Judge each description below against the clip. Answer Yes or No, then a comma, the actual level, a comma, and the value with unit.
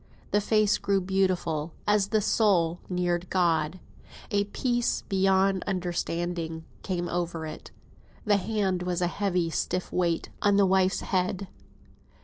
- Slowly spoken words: Yes, slow, 130 wpm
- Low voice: No, medium, 185 Hz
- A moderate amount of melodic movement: No, narrow, 2.3 semitones